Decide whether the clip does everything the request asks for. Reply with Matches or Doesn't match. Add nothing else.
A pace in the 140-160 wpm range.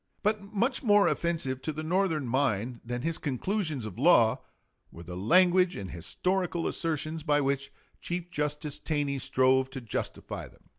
Matches